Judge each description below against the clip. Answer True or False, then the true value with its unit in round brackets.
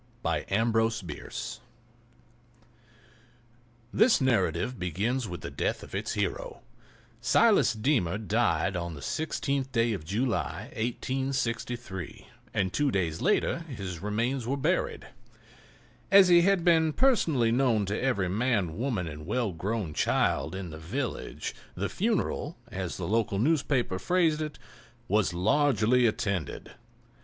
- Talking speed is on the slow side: True (130 wpm)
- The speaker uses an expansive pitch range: True (6.2 semitones)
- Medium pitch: False (115 Hz)